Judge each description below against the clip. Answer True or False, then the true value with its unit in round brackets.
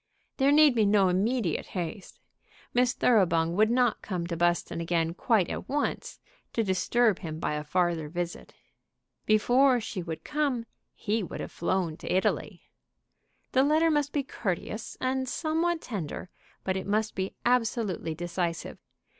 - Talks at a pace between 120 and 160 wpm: True (150 wpm)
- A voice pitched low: False (205 Hz)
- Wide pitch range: True (6.3 semitones)